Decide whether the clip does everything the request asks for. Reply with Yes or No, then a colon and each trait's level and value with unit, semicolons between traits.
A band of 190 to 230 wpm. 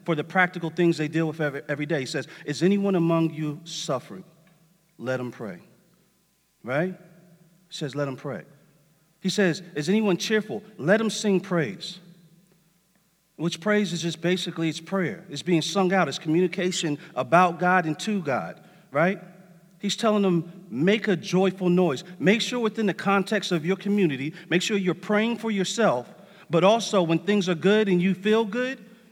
No: average, 175 wpm